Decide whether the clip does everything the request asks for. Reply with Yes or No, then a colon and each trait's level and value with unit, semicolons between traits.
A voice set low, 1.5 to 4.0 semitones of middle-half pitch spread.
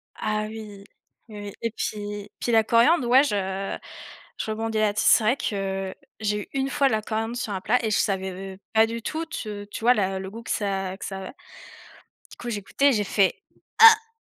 No: high, 215 Hz; average, 2.9 semitones